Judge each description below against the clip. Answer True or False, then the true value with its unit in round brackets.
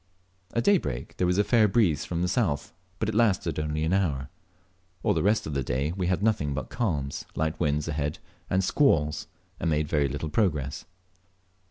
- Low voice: True (80 Hz)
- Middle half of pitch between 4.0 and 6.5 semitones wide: True (5.2 semitones)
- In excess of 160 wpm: True (190 wpm)